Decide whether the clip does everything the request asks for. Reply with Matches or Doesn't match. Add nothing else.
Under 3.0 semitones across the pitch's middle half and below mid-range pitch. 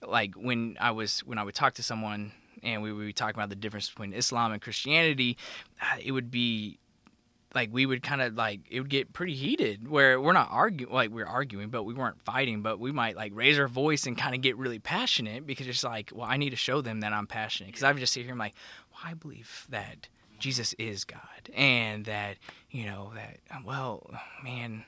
Doesn't match